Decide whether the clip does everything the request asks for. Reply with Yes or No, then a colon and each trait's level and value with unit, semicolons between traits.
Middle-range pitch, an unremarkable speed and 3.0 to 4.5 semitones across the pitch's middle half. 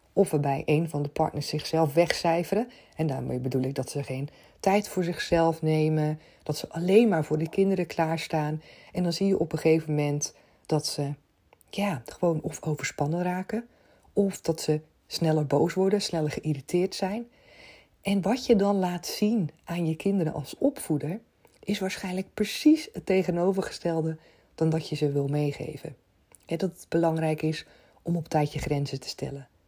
Yes: medium, 165 Hz; average, 170 wpm; average, 3.9 semitones